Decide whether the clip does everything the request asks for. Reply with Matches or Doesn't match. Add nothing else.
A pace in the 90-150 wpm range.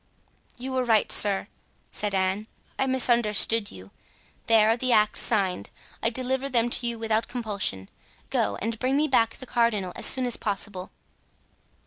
Doesn't match